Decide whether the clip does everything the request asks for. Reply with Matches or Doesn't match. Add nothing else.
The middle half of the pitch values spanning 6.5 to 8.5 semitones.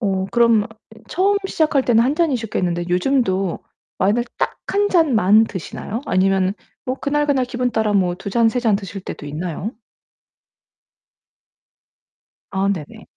Doesn't match